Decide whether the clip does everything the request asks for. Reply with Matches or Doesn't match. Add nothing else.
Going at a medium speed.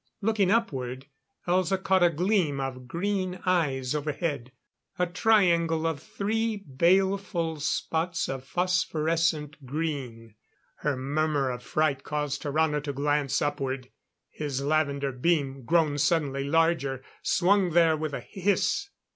Doesn't match